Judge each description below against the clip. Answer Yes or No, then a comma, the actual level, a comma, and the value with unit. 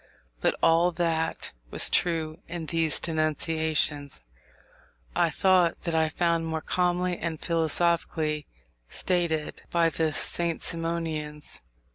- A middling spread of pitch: No, narrow, 1.4 semitones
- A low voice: No, medium, 165 Hz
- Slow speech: Yes, slow, 110 wpm